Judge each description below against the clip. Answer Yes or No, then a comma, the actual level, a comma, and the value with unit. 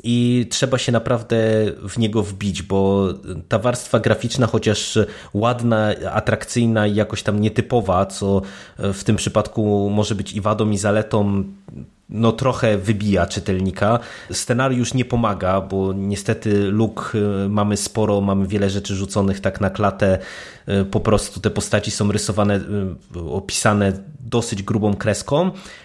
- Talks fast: No, average, 130 wpm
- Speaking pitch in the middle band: No, low, 105 Hz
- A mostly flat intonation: Yes, narrow, 2.3 semitones